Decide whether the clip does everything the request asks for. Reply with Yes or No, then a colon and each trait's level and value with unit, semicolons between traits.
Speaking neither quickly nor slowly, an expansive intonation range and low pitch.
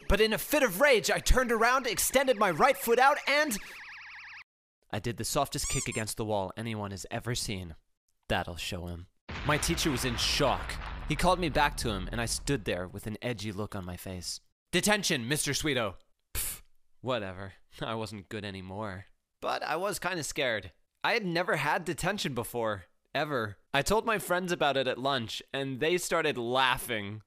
Yes: average, 190 wpm; wide, 9.0 semitones; low, 125 Hz